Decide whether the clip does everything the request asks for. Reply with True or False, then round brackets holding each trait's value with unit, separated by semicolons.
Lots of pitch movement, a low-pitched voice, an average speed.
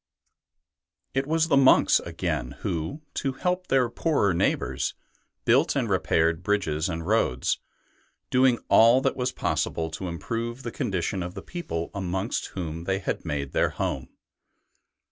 True (7.7 semitones; 100 Hz; 145 wpm)